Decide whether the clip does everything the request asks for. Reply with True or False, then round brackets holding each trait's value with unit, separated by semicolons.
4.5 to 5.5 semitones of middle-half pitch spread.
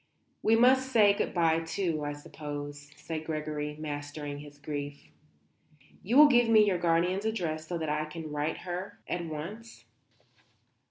True (5.0 semitones)